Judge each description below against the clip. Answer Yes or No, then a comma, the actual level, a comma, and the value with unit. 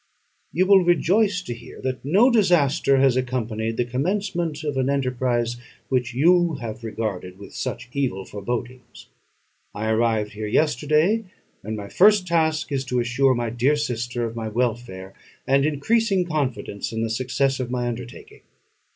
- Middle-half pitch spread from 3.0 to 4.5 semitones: No, average, 5.0 semitones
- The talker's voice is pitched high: No, low, 130 Hz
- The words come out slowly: No, average, 155 wpm